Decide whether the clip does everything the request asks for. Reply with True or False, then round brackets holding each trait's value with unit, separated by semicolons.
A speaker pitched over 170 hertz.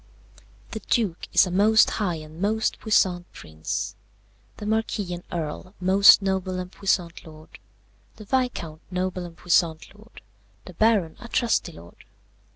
True (185 Hz)